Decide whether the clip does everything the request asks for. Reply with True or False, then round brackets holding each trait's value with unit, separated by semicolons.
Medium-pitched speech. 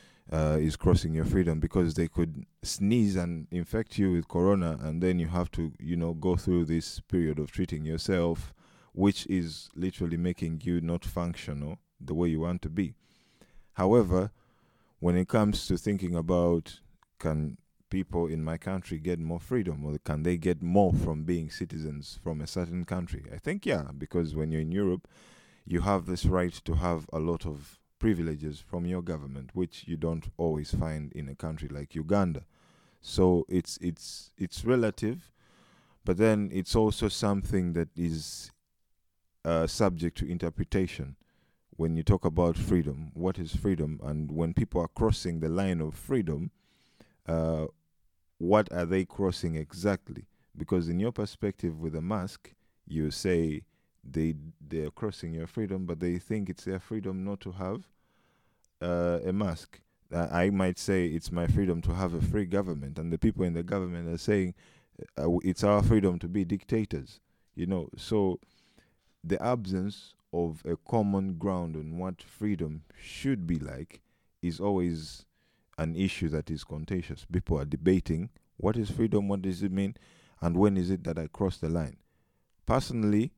False (85 Hz)